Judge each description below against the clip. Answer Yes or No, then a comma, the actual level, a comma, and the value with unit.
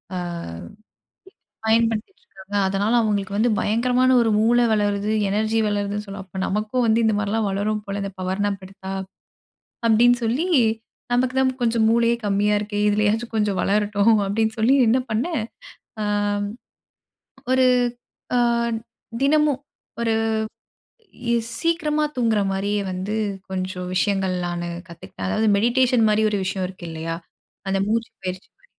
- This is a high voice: Yes, high, 210 Hz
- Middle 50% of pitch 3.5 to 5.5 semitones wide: No, average, 2.7 semitones